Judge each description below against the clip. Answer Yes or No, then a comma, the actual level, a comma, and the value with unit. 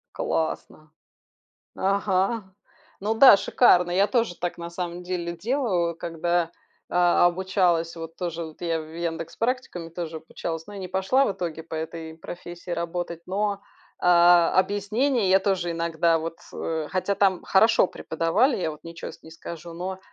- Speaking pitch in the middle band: Yes, medium, 175 Hz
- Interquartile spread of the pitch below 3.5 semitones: Yes, average, 2.7 semitones